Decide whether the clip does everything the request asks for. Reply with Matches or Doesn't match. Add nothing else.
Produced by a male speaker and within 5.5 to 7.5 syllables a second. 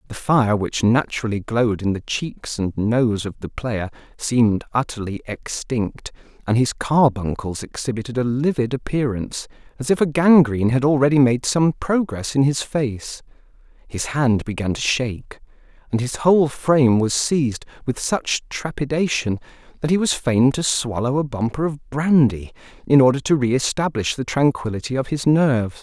Doesn't match